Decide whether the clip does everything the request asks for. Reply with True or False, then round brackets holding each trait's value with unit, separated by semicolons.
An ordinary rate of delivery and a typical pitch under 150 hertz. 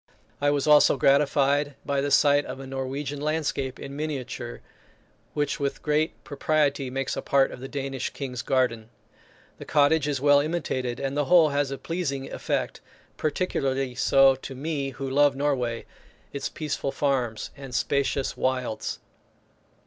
True (150 wpm; 140 Hz)